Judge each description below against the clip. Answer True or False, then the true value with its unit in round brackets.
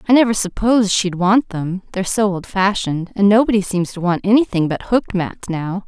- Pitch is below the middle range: False (195 Hz)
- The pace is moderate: True (185 wpm)